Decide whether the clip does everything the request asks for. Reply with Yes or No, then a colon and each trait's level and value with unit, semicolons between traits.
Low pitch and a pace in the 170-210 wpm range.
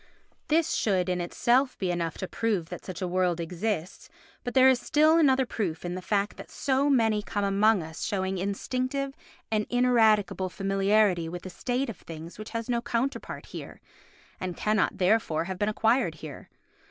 No: high, 205 Hz; average, 175 wpm